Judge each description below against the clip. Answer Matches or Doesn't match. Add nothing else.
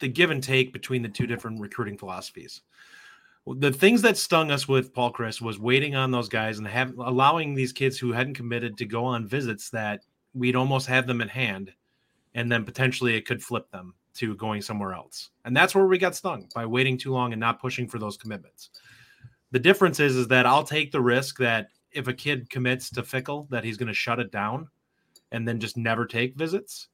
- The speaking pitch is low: Matches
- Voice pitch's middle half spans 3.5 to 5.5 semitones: Doesn't match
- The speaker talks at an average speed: Doesn't match